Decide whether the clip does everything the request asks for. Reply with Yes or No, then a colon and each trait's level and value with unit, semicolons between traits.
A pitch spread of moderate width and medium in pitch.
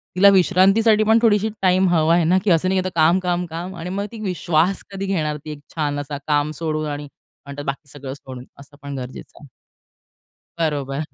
Yes: average, 4.4 semitones; medium, 165 Hz